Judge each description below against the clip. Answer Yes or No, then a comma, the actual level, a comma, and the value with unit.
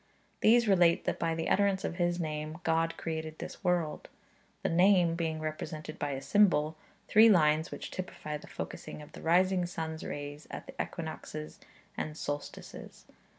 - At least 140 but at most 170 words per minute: Yes, average, 165 wpm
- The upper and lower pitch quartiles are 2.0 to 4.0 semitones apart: Yes, narrow, 2.5 semitones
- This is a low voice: No, medium, 165 Hz